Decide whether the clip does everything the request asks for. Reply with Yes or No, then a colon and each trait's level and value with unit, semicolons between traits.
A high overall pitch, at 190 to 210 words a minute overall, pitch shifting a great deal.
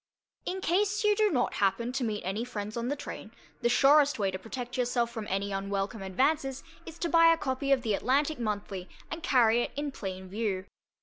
Yes: high, 240 Hz; fast, 205 wpm; wide, 6.1 semitones